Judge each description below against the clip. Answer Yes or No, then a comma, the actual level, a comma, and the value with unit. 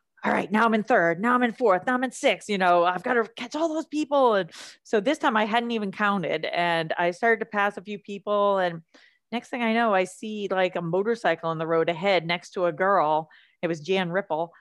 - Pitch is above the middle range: Yes, high, 200 Hz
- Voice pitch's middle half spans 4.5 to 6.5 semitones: Yes, average, 4.9 semitones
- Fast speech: Yes, fast, 250 wpm